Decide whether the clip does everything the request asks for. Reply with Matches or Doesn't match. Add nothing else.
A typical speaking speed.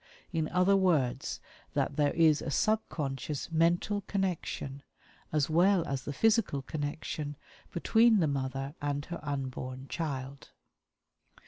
Doesn't match